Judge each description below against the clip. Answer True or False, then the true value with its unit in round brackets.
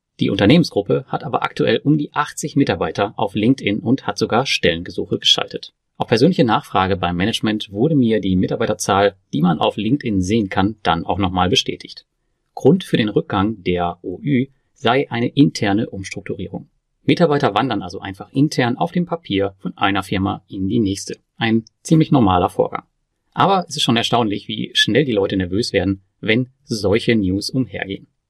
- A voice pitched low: True (115 Hz)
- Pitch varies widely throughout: True (5.8 semitones)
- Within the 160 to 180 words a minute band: True (165 wpm)